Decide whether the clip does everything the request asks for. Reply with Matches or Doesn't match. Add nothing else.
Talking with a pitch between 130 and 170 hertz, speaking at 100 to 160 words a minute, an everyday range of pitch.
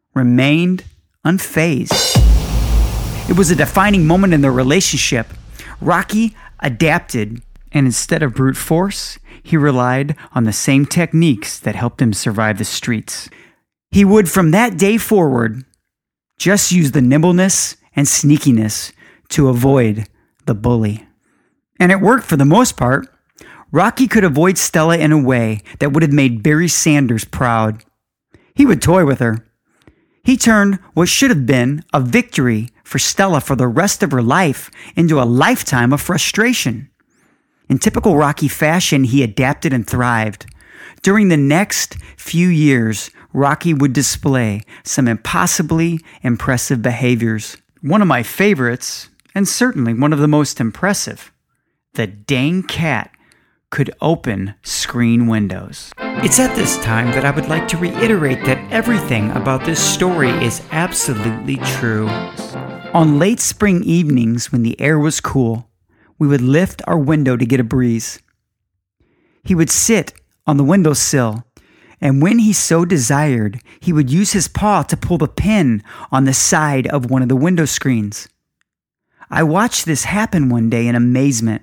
Doesn't match